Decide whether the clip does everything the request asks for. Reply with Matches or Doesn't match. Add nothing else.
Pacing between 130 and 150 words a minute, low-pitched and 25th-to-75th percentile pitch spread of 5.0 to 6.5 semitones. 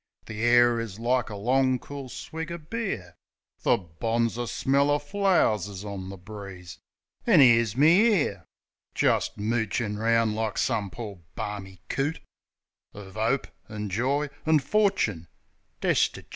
Matches